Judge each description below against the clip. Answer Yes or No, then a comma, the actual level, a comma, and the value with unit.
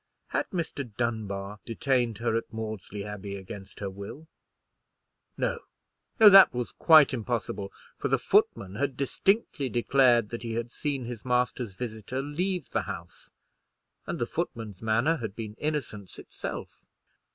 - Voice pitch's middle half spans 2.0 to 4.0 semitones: No, average, 4.7 semitones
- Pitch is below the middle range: Yes, low, 115 Hz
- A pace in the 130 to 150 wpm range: Yes, average, 140 wpm